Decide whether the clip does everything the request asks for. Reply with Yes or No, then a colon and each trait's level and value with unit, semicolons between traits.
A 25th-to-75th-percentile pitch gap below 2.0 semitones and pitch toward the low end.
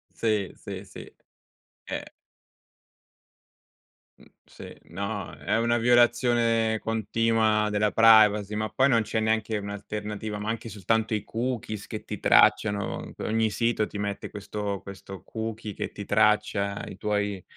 Yes: narrow, 1.6 semitones; low, 110 Hz